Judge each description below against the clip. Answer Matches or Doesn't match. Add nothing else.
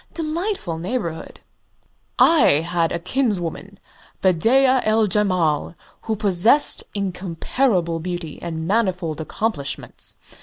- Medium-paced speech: Doesn't match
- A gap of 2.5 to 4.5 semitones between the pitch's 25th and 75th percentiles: Doesn't match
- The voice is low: Doesn't match